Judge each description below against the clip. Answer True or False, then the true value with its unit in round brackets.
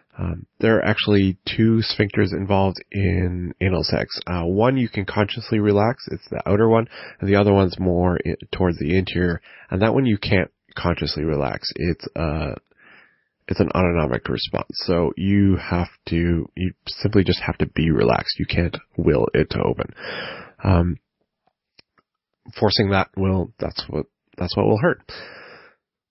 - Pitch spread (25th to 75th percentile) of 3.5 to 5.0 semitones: False (3.1 semitones)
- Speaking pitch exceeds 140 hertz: False (95 Hz)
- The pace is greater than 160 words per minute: False (155 wpm)